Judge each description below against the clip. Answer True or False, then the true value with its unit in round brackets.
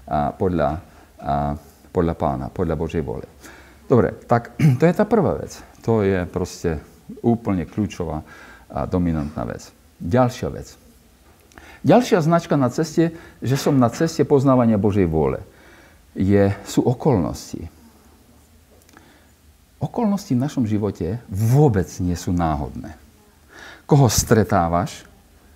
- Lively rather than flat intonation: True (7.4 semitones)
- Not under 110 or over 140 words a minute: True (115 wpm)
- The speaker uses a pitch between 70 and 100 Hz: True (95 Hz)